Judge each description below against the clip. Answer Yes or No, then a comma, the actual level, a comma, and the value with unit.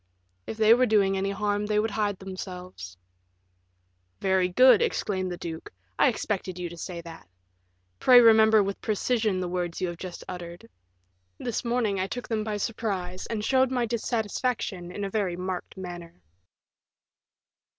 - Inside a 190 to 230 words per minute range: No, average, 160 wpm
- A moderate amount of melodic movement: Yes, average, 3.4 semitones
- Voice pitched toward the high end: Yes, high, 200 Hz